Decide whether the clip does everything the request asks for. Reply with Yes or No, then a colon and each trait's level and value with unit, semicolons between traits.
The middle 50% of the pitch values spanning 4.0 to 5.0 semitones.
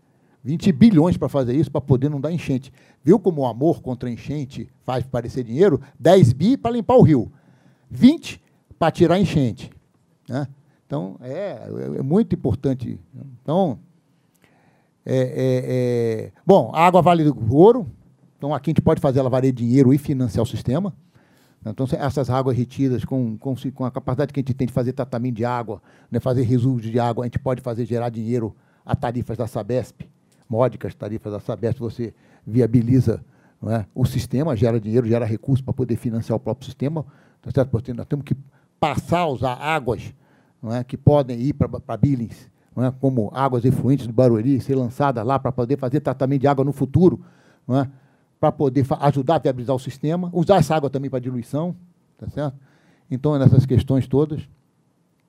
No: average, 3.3 semitones